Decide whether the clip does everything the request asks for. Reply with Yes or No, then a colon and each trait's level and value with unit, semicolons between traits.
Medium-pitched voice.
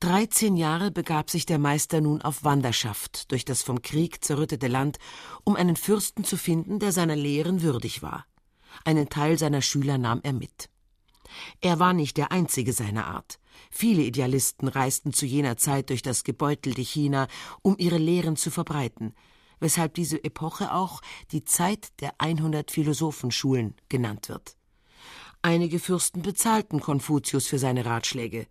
Yes: medium, 150 Hz